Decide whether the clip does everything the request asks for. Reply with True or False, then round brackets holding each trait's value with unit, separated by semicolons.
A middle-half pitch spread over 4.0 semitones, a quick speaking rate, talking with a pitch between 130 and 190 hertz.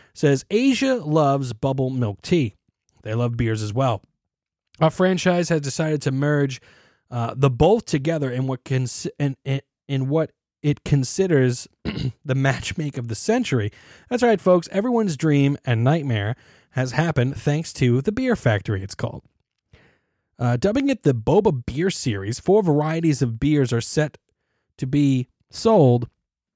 False (4.8 semitones; 150 wpm; 140 Hz)